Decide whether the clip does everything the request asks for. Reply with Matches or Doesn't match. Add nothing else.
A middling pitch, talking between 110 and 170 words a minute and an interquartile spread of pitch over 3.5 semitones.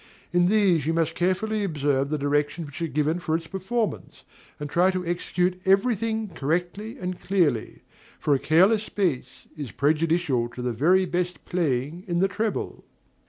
Matches